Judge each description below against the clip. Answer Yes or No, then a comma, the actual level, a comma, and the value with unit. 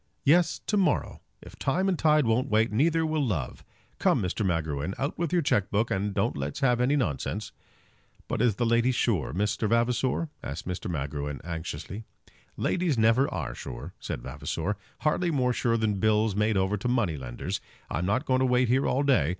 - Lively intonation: Yes, wide, 6.4 semitones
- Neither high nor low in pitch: No, low, 115 Hz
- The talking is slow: No, average, 190 wpm